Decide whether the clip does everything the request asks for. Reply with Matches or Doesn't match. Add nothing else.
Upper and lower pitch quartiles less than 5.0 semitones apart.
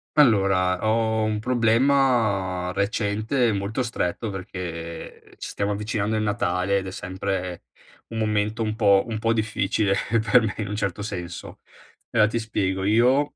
Matches